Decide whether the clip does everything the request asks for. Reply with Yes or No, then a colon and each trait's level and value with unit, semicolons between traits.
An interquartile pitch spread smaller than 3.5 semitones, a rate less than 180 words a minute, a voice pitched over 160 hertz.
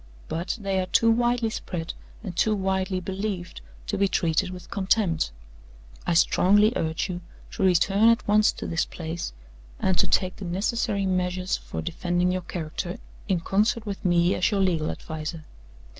Yes: average, 2.8 semitones; average, 165 wpm; medium, 185 Hz